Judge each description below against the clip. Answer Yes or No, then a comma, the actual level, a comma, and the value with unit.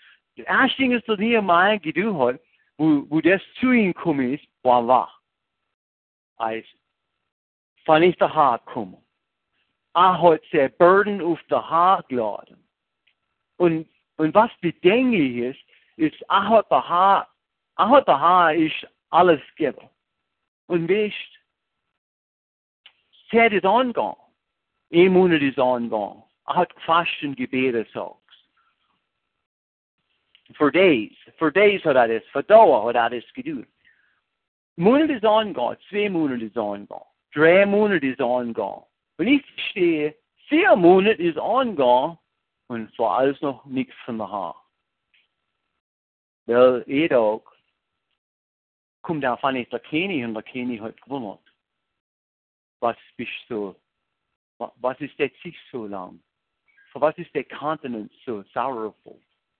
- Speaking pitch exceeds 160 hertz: No, medium, 155 Hz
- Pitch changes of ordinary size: No, wide, 8.9 semitones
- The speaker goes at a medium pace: No, slow, 105 wpm